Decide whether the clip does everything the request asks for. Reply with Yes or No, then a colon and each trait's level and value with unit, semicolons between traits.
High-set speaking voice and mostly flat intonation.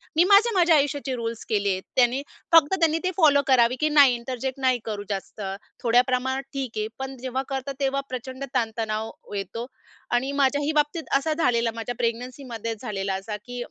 No: very high, 255 Hz; average, 3.5 semitones